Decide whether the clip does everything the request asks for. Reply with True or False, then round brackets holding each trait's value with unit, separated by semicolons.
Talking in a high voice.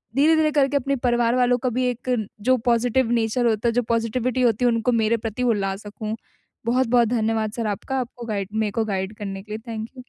True (230 Hz)